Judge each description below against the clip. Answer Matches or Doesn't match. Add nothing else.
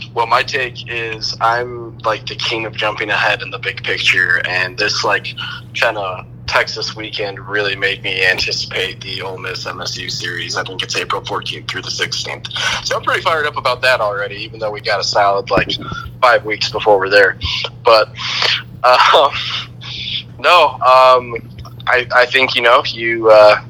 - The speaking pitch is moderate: Doesn't match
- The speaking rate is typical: Matches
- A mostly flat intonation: Matches